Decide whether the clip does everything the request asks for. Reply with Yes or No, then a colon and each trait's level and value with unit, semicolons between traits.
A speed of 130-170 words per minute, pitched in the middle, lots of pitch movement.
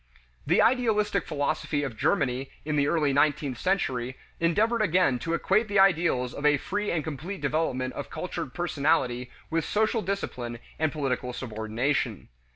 Yes: average, 150 wpm; medium, 150 Hz; wide, 6.4 semitones